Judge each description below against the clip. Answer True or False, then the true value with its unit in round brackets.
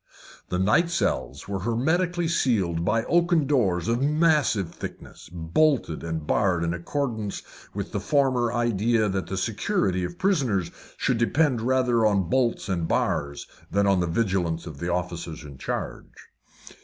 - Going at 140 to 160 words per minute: True (150 wpm)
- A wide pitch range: True (7.1 semitones)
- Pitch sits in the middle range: False (110 Hz)